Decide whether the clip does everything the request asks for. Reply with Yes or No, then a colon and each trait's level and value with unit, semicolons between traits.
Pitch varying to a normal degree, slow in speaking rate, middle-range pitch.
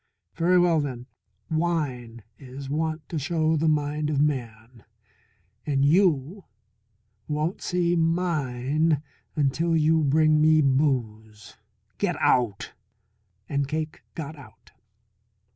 Yes: average, 3.4 semitones; slow, 110 wpm; medium, 150 Hz